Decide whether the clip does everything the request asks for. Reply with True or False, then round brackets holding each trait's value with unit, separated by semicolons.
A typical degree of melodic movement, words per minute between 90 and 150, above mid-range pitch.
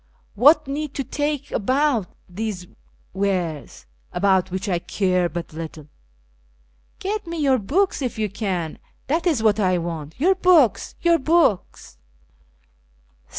False (8.5 semitones; 135 wpm; 220 Hz)